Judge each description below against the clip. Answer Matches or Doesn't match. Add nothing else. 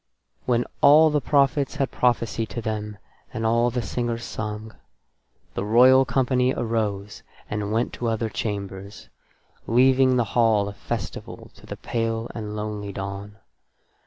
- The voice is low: Matches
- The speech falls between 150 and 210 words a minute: Doesn't match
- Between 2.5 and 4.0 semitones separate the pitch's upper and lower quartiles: Matches